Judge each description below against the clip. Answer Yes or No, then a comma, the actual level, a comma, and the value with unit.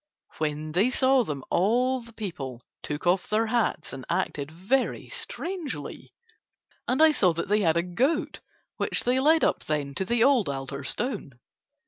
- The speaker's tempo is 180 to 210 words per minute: No, average, 165 wpm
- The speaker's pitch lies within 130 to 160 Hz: No, high, 205 Hz